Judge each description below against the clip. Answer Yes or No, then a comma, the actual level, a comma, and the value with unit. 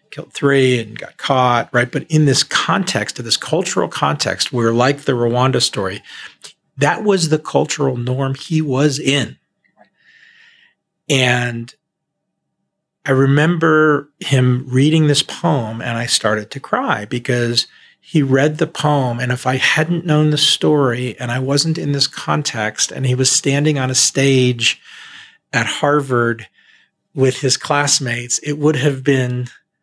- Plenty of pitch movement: No, average, 3.3 semitones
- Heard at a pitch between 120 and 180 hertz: Yes, low, 135 Hz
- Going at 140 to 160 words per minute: Yes, average, 145 wpm